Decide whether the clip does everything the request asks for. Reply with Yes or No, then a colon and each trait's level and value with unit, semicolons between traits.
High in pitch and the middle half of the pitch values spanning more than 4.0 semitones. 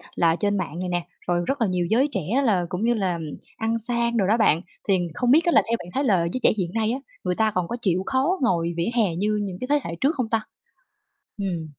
Yes: high, 205 Hz; average, 5.1 semitones